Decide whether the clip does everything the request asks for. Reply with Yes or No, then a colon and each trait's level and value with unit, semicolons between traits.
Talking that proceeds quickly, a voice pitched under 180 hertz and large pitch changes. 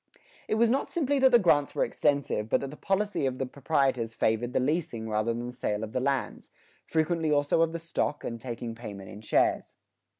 Yes: fast, 220 wpm; low, 135 Hz; wide, 6.0 semitones